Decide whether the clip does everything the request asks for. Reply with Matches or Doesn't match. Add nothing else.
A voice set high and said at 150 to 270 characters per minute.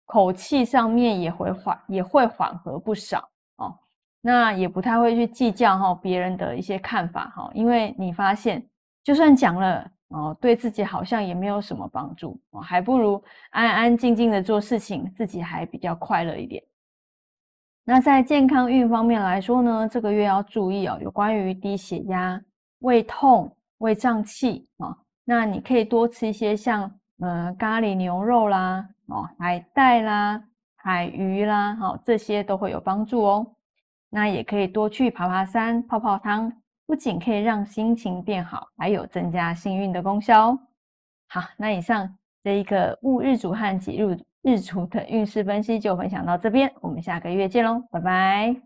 Matches